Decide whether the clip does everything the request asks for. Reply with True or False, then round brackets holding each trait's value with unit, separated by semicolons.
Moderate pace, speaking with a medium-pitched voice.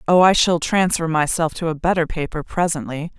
True (190 wpm; 165 Hz)